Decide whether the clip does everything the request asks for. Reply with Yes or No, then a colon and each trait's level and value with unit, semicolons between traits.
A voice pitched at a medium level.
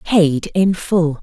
Yes: medium, 170 Hz